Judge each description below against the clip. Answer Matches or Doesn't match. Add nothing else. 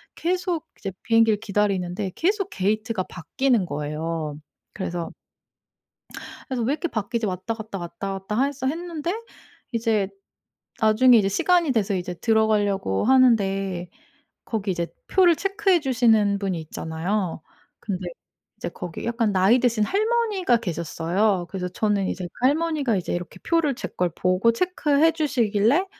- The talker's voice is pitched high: Matches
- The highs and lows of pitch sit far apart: Matches